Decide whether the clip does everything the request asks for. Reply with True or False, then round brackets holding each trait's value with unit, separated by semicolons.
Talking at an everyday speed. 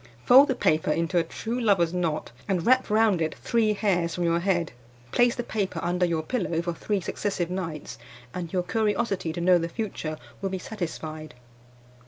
True (185 wpm)